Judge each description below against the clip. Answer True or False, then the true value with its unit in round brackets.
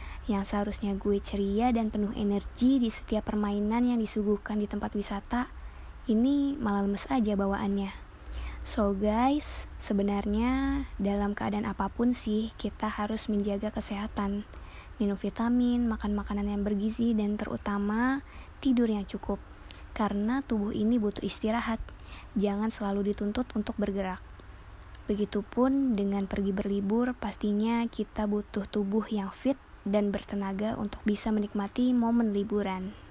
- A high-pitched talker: True (210 Hz)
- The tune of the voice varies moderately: False (2.0 semitones)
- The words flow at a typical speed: True (125 wpm)